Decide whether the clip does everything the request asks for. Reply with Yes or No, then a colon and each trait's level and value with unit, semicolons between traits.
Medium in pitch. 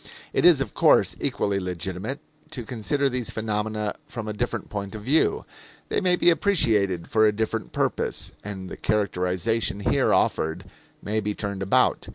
No: low, 105 Hz